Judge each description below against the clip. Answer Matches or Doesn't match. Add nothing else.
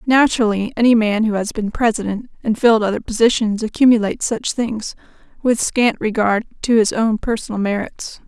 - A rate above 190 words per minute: Doesn't match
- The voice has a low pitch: Doesn't match